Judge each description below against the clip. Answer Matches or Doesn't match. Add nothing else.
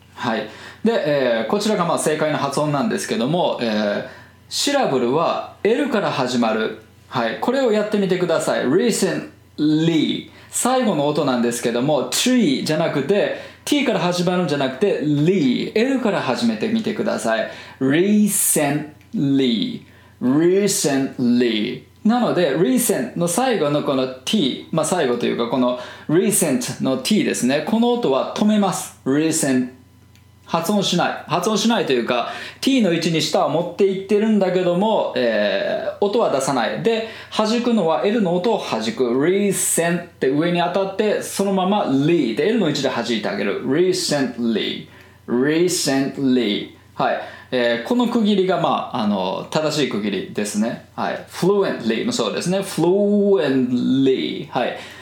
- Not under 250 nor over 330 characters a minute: Doesn't match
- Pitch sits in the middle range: Matches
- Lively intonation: Matches